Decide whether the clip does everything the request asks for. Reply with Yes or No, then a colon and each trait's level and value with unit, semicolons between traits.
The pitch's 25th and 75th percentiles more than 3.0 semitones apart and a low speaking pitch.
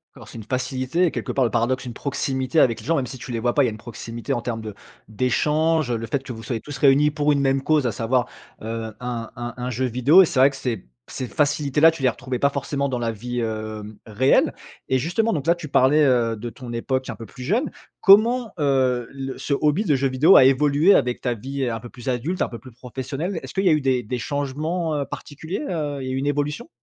Yes: average, 3.5 semitones; low, 130 Hz